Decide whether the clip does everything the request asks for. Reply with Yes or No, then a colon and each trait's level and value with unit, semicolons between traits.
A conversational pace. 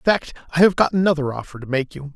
No: fast, 280 wpm